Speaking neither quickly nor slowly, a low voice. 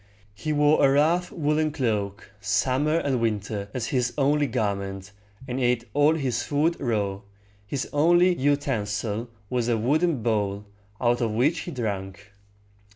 Yes: average, 145 wpm; low, 125 Hz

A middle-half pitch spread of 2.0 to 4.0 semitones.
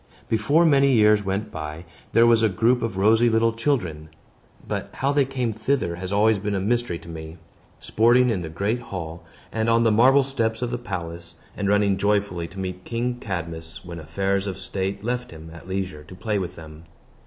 No: average, 4.9 semitones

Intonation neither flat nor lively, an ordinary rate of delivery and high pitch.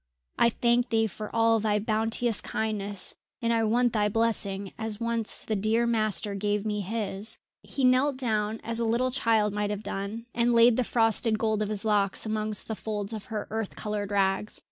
No: narrow, 1.8 semitones; average, 190 wpm; high, 220 Hz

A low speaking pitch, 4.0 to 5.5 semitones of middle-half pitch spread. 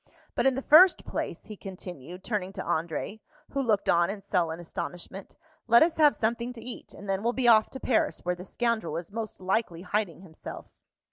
No: high, 200 Hz; average, 4.8 semitones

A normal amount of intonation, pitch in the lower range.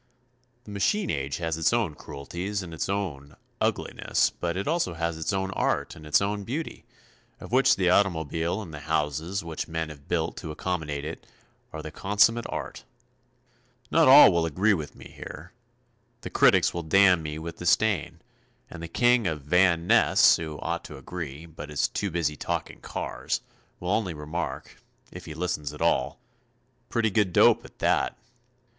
Yes: average, 4.0 semitones; very low, 85 Hz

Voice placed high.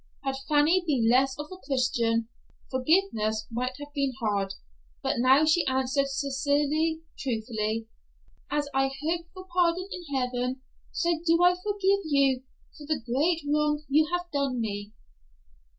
Yes: very high, 280 Hz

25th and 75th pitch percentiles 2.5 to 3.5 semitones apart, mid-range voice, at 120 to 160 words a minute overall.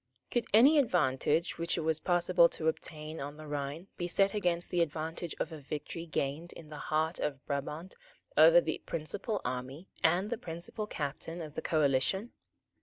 No: average, 3.0 semitones; medium, 160 Hz; average, 175 wpm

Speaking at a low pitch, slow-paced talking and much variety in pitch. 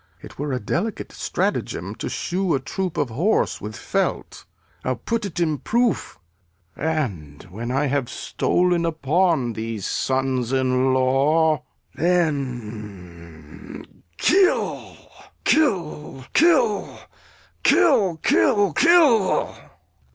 No: medium, 150 Hz; slow, 100 wpm; wide, 6.8 semitones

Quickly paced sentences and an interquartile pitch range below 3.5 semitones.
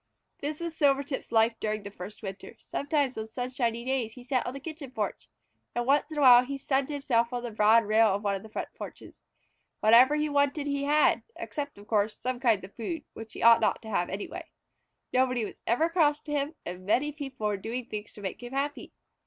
No: fast, 225 wpm; average, 4.6 semitones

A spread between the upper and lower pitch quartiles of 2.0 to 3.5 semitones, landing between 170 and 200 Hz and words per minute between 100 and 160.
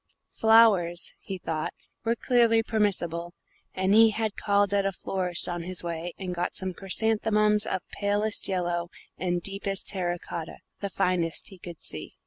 Yes: average, 3.2 semitones; high, 190 Hz; average, 155 wpm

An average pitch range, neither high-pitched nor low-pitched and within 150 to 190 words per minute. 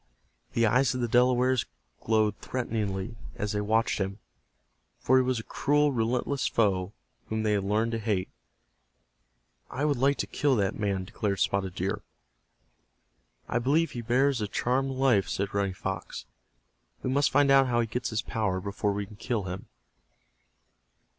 No: average, 4.1 semitones; low, 115 Hz; average, 165 wpm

